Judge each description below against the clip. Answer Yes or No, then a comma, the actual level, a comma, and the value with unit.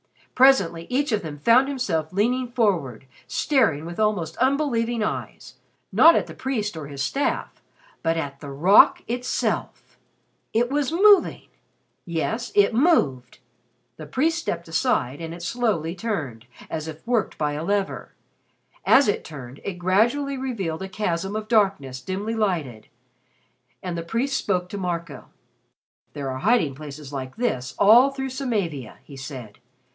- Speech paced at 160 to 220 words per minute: No, average, 150 wpm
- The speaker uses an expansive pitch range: Yes, wide, 7.9 semitones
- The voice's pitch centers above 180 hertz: Yes, high, 190 Hz